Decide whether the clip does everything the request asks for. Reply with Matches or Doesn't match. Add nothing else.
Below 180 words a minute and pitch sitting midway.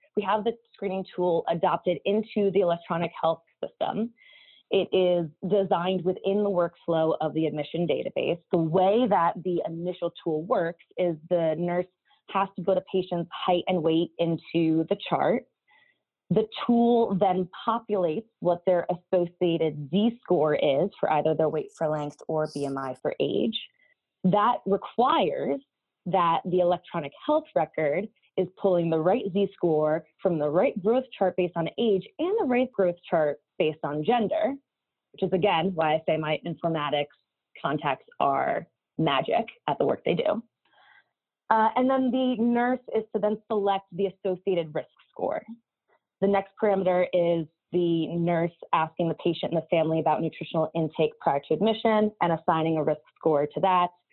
Matches